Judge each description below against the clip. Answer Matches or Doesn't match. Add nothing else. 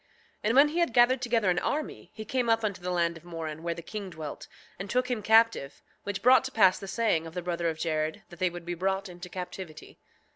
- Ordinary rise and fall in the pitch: Matches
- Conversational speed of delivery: Doesn't match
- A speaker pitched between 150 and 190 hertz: Matches